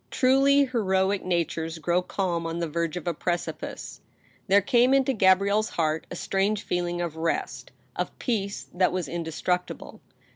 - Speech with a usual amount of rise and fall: Yes, average, 3.2 semitones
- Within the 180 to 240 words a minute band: No, average, 150 wpm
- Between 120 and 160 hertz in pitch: No, medium, 180 Hz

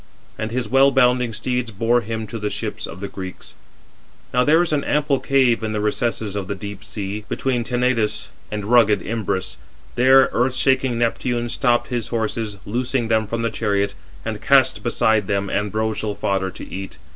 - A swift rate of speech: No, average, 180 wpm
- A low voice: Yes, low, 115 Hz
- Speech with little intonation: No, average, 3.1 semitones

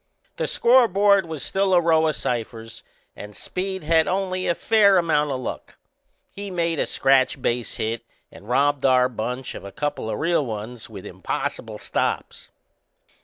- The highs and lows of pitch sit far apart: Yes, wide, 7.0 semitones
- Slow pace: No, average, 165 wpm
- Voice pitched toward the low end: No, medium, 150 Hz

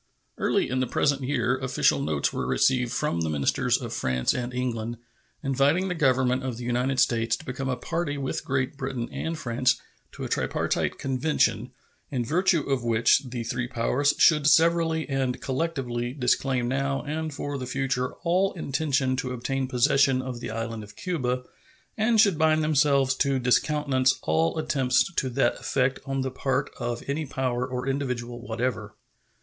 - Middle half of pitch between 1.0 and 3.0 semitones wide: Yes, narrow, 2.6 semitones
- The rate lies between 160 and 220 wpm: Yes, average, 170 wpm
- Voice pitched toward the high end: No, low, 130 Hz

